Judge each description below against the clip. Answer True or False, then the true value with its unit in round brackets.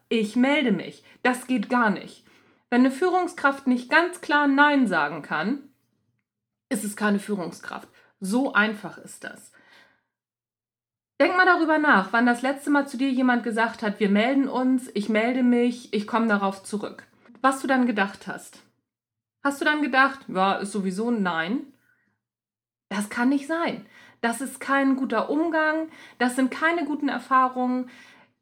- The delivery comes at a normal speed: True (160 wpm)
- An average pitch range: True (4.9 semitones)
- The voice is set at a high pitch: True (245 Hz)